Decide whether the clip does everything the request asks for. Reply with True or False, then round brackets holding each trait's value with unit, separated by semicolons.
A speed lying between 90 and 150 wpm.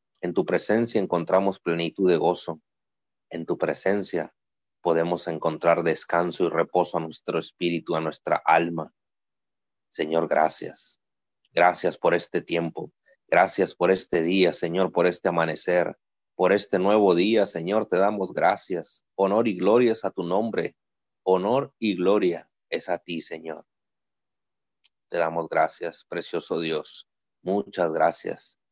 True (135 wpm)